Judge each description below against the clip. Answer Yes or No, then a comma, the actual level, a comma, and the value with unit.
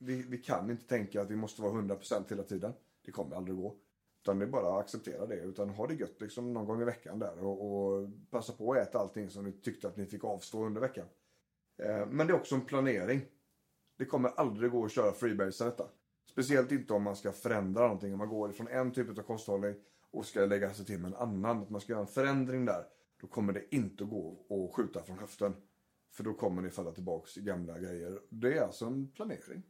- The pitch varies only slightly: No, average, 3.5 semitones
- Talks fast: Yes, fast, 240 wpm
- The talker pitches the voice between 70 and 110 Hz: Yes, low, 105 Hz